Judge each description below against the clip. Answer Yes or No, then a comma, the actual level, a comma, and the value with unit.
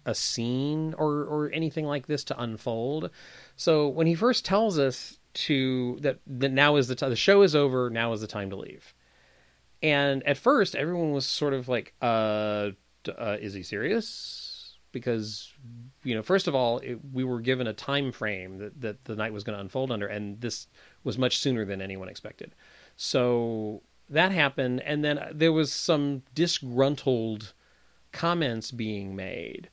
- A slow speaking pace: No, average, 175 wpm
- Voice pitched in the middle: No, low, 130 Hz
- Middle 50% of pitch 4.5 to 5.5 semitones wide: Yes, average, 5.0 semitones